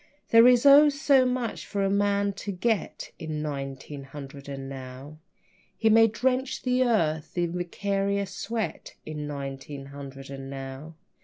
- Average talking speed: Yes, average, 150 wpm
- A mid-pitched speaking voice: Yes, medium, 170 Hz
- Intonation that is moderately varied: No, wide, 8.4 semitones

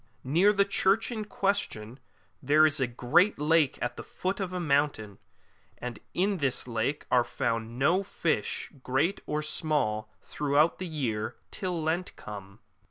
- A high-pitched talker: No, medium, 150 Hz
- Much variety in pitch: Yes, wide, 6.8 semitones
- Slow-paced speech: No, average, 155 wpm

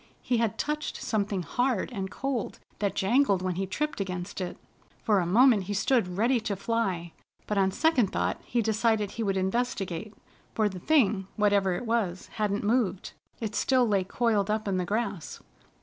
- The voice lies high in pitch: Yes, high, 210 Hz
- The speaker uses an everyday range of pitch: Yes, average, 3.6 semitones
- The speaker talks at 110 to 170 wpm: No, average, 180 wpm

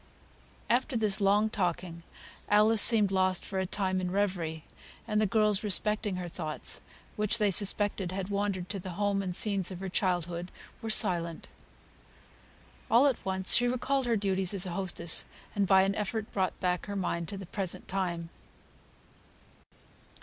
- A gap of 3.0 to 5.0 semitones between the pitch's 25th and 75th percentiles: No, narrow, 2.5 semitones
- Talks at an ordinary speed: Yes, average, 160 wpm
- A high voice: Yes, high, 195 Hz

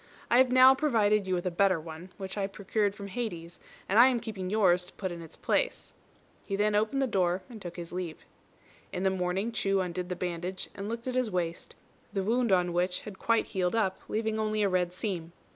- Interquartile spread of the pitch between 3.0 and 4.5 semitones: Yes, average, 3.5 semitones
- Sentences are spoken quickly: Yes, fast, 225 wpm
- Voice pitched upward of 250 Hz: No, high, 195 Hz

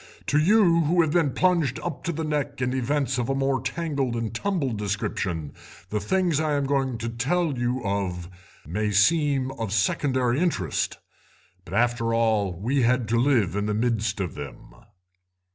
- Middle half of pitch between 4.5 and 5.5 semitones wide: Yes, average, 5.2 semitones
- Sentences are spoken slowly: No, average, 175 wpm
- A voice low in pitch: Yes, low, 125 Hz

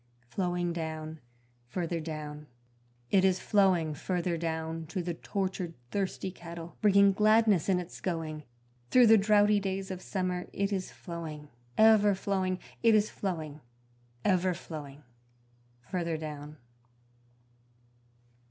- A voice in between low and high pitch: Yes, medium, 180 Hz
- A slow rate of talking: Yes, slow, 120 wpm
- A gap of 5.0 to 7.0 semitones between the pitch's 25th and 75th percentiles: No, average, 3.3 semitones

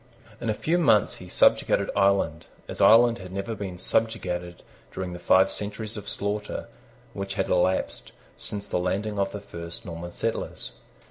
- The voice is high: No, low, 100 Hz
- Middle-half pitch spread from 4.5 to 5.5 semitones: No, average, 2.8 semitones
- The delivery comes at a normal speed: Yes, average, 160 wpm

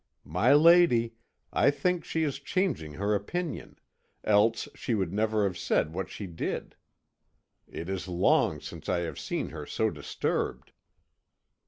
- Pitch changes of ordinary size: No, wide, 8.1 semitones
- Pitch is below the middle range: Yes, low, 105 Hz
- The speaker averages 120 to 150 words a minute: Yes, average, 145 wpm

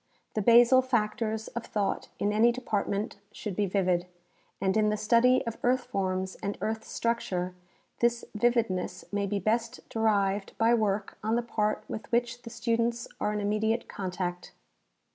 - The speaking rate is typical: Yes, average, 160 wpm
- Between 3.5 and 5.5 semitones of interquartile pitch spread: No, average, 2.8 semitones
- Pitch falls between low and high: No, high, 215 Hz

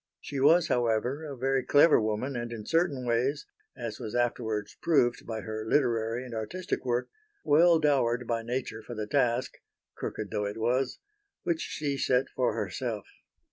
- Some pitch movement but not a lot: Yes, average, 3.7 semitones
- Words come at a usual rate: Yes, average, 165 wpm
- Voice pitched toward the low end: Yes, low, 120 Hz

